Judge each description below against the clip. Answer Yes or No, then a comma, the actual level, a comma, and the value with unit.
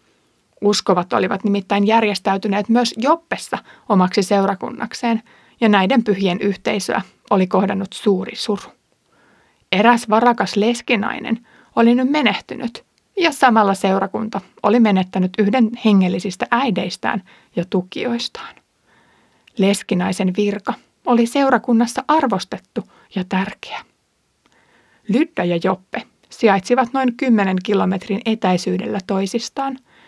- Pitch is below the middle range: No, high, 210 Hz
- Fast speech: No, slow, 95 wpm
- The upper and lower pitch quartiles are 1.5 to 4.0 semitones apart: Yes, average, 3.5 semitones